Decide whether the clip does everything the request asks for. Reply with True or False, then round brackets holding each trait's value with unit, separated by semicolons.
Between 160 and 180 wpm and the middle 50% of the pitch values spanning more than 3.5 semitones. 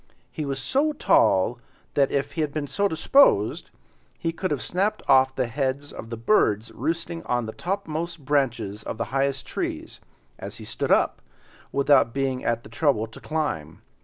True (175 wpm; 5.3 semitones)